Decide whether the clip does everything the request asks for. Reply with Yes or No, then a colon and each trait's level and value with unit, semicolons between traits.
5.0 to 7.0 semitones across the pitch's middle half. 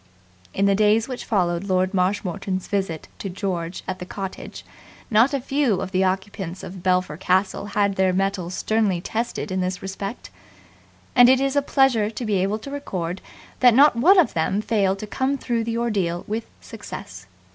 No: average, 3.7 semitones